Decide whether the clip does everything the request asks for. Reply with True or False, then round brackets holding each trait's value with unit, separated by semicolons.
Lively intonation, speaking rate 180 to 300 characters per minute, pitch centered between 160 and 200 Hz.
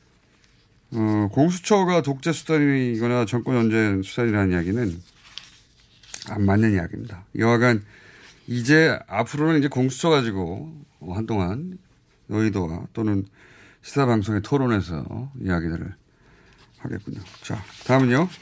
False (5.9 semitones; 270 characters per minute; 115 Hz)